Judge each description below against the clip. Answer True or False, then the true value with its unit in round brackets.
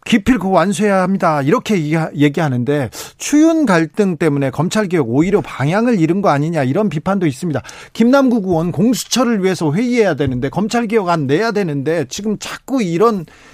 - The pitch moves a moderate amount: False (6.2 semitones)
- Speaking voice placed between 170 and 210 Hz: True (185 Hz)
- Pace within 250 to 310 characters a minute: False (375 characters per minute)